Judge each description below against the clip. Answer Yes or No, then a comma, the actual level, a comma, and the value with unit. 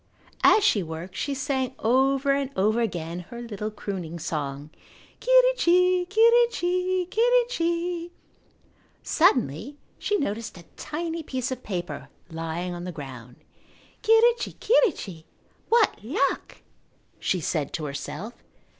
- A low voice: No, very high, 255 Hz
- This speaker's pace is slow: Yes, slow, 115 wpm